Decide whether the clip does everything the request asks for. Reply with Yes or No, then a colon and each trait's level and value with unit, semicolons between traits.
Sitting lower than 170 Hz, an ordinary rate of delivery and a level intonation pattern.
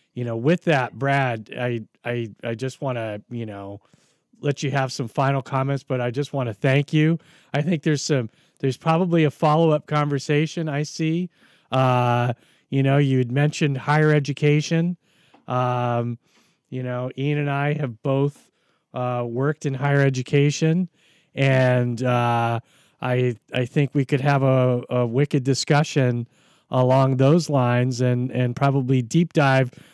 No: low, 135 Hz; average, 155 wpm; average, 3.1 semitones